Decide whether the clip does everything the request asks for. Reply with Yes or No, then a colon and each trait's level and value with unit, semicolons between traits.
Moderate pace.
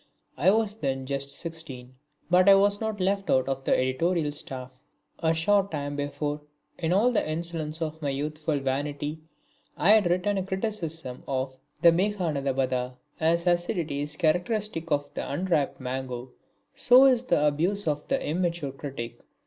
Yes: average, 155 wpm